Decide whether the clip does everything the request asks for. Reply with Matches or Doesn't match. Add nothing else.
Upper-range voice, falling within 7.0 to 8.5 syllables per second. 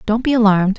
Matches